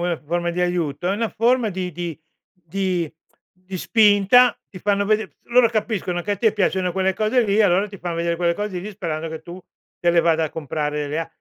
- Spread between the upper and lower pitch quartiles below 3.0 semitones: No, average, 3.4 semitones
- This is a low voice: No, medium, 180 Hz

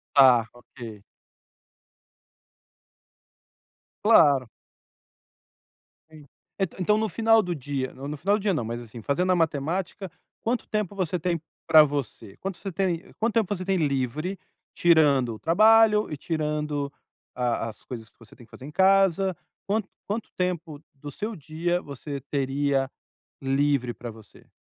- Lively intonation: Yes, wide, 6.0 semitones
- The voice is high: No, medium, 155 Hz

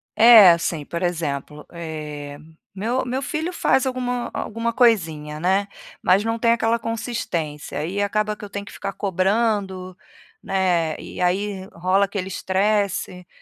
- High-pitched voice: Yes, high, 195 Hz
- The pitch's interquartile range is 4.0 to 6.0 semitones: Yes, average, 4.7 semitones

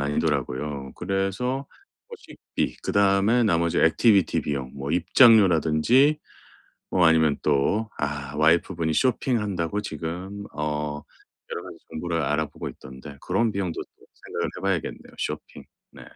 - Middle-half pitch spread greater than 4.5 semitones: Yes, average, 5.3 semitones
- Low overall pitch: Yes, very low, 85 Hz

